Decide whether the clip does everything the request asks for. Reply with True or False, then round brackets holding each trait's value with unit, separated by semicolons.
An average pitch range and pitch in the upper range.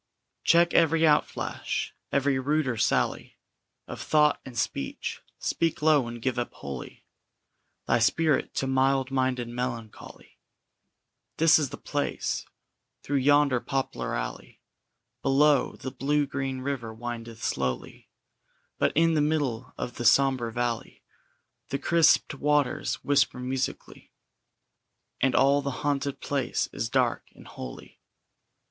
False (3.2 semitones; 135 Hz)